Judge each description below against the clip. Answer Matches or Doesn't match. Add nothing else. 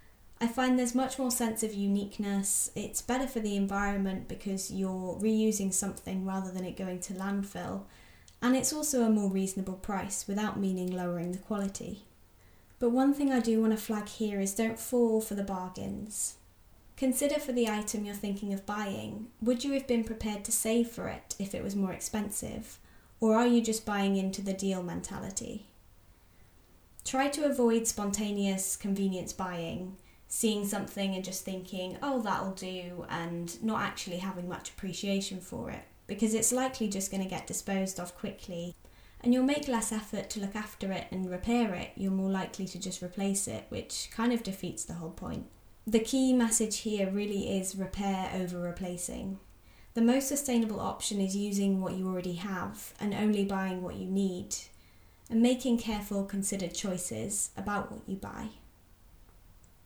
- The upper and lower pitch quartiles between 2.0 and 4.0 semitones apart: Matches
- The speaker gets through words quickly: Doesn't match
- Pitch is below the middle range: Doesn't match